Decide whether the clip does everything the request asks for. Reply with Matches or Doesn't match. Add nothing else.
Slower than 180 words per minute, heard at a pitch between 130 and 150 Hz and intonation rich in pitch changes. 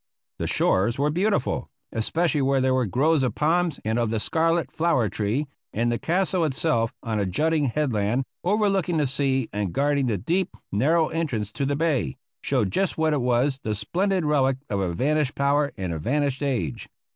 Doesn't match